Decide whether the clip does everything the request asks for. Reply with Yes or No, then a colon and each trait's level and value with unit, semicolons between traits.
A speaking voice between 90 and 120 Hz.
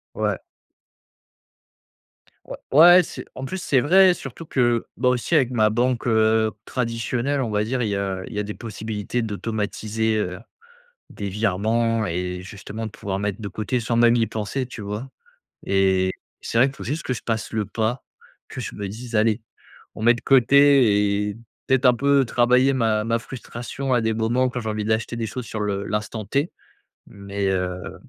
Yes: low, 115 Hz